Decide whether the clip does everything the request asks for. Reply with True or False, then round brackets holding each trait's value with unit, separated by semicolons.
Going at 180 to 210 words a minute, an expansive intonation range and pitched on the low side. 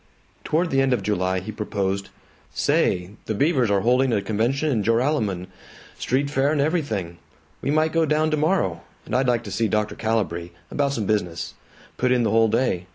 True (185 wpm; 5.8 semitones; 115 Hz)